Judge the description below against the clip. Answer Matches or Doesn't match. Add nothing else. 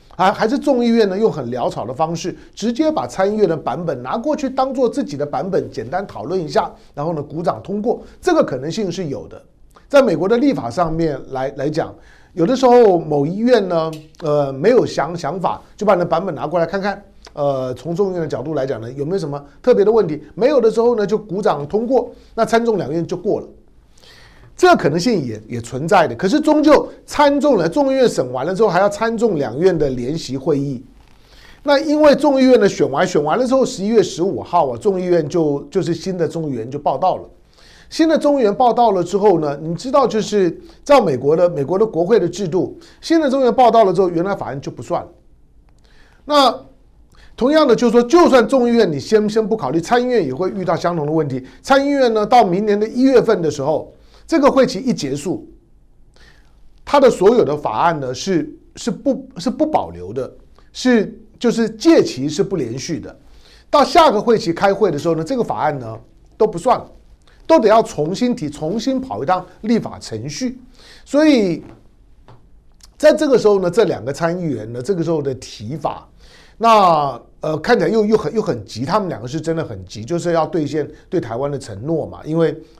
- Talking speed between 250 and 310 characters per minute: Matches